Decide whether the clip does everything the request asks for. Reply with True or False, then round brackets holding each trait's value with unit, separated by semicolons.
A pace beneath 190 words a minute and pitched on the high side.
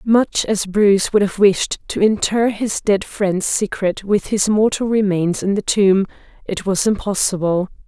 True (170 wpm; 200 Hz)